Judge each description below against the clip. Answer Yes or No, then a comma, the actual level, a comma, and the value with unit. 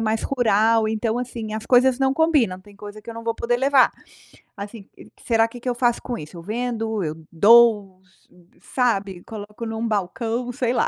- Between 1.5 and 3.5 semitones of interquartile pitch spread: Yes, average, 2.9 semitones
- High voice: Yes, high, 225 Hz